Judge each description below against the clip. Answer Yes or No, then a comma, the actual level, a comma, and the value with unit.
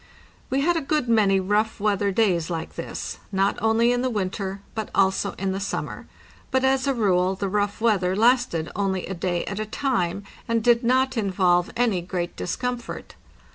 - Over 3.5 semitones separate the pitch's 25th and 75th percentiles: Yes, average, 4.1 semitones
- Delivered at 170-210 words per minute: Yes, average, 180 wpm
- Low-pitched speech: No, high, 205 Hz